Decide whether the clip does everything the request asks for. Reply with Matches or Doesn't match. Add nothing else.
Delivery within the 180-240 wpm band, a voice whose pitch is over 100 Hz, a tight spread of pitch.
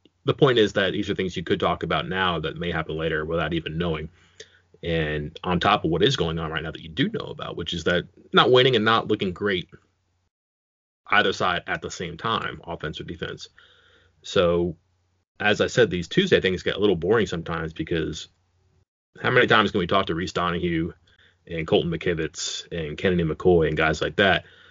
Doesn't match